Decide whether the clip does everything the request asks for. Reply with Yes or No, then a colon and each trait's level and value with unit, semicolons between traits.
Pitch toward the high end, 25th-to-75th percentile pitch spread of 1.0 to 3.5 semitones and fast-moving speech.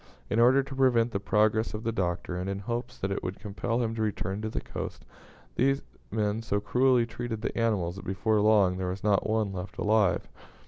No: low, 110 Hz; average, 2.9 semitones; fast, 215 wpm